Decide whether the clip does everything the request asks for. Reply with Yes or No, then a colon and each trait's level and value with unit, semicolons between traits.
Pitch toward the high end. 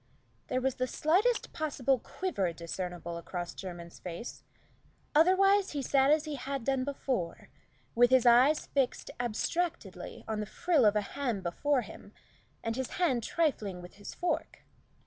Yes: very high, 255 Hz